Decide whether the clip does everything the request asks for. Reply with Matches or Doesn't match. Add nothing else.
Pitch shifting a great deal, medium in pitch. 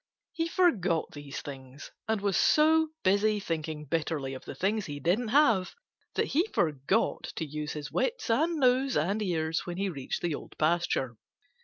Matches